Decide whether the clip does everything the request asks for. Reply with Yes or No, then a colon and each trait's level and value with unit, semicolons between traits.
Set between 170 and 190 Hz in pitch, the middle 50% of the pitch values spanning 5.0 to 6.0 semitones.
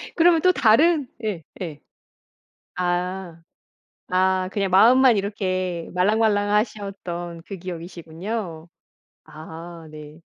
No: medium, 185 Hz; average, 3.8 semitones